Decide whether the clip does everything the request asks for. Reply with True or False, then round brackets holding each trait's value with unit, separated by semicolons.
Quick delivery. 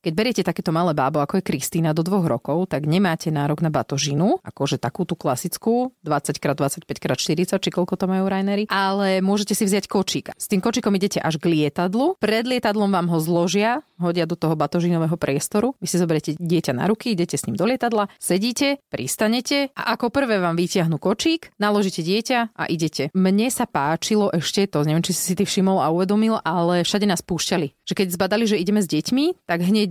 True (195 wpm)